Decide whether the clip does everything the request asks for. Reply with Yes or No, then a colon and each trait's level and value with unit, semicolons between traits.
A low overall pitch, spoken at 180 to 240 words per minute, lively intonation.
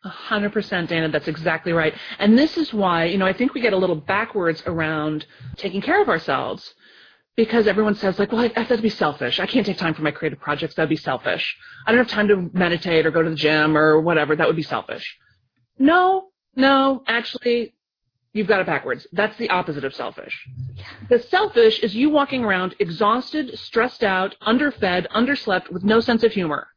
No: high, 195 Hz; fast, 205 wpm; wide, 6.6 semitones